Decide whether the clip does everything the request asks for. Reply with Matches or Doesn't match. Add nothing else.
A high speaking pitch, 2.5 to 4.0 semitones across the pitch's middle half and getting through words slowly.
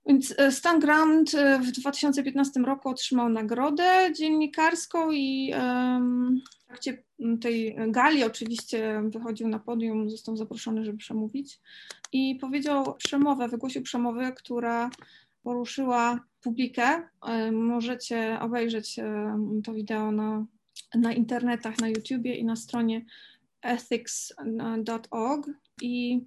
Matches